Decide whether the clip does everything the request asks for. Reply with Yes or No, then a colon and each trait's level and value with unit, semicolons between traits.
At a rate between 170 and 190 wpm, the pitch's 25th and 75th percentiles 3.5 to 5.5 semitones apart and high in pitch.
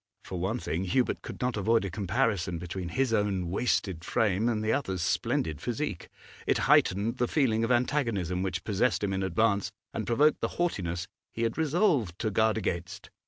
No: average, 180 wpm; average, 4.5 semitones; low, 105 Hz